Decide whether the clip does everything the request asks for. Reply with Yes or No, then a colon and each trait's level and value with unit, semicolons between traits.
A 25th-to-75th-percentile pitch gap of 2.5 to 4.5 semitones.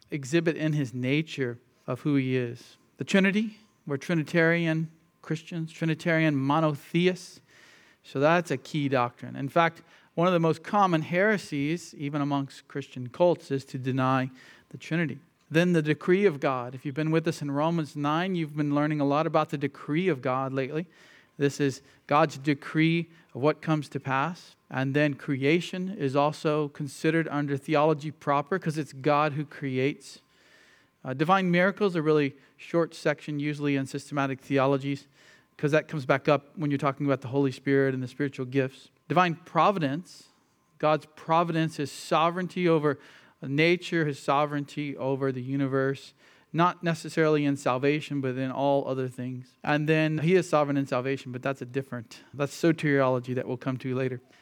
Yes: average, 2.9 semitones